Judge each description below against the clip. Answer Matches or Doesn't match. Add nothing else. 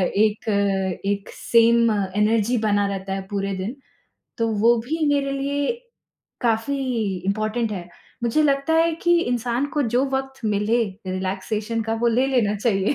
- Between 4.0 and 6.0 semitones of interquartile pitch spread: Matches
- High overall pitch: Matches